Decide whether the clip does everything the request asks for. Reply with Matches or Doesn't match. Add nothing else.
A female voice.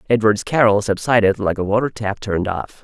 Doesn't match